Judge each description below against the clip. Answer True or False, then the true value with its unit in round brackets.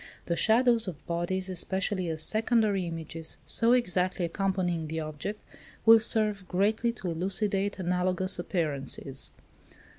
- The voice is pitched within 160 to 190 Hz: True (185 Hz)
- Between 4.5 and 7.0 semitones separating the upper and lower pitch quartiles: False (3.7 semitones)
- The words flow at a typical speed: False (120 wpm)